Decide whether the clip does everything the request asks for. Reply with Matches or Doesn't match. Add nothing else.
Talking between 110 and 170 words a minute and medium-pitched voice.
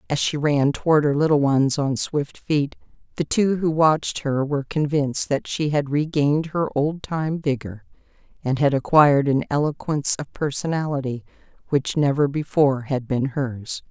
Matches